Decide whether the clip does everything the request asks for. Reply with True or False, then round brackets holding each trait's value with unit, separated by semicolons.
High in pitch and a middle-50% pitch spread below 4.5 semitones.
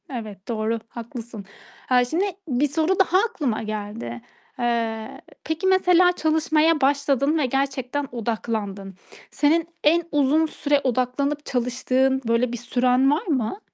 False (265 Hz; 4.8 semitones)